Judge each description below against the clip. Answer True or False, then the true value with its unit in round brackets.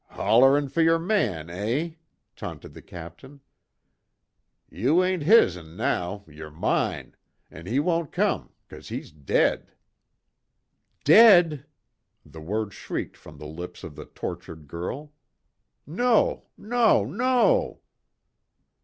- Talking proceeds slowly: True (115 wpm)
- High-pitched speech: False (130 Hz)